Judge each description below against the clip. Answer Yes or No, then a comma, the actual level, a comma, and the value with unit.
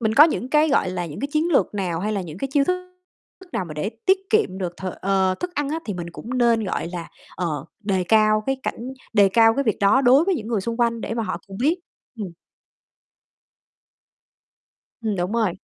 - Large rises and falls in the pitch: Yes, wide, 6.2 semitones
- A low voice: No, high, 220 Hz